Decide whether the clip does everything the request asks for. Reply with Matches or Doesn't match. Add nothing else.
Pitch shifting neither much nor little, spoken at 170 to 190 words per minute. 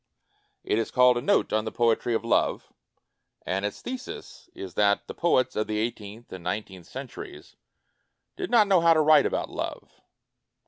Doesn't match